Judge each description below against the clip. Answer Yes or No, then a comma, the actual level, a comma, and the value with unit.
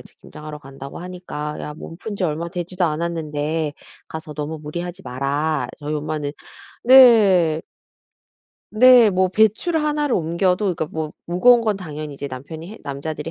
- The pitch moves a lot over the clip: No, average, 3.9 semitones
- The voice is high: No, medium, 160 Hz